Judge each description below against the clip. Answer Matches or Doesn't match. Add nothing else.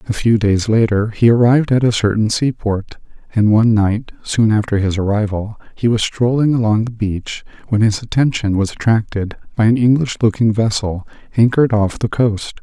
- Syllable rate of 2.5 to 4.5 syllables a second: Doesn't match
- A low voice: Matches